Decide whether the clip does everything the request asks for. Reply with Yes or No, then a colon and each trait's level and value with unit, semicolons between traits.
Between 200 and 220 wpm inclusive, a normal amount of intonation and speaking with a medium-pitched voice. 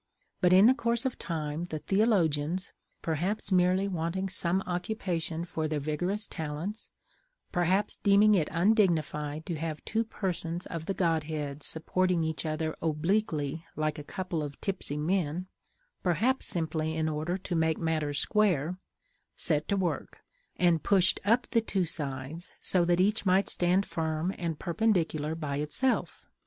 No: average, 145 wpm; average, 3.5 semitones; medium, 170 Hz